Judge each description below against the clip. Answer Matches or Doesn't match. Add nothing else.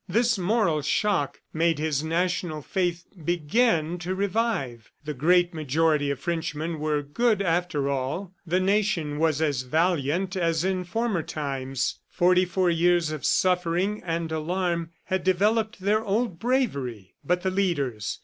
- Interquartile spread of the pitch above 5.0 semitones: Doesn't match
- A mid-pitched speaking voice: Matches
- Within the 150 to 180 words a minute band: Doesn't match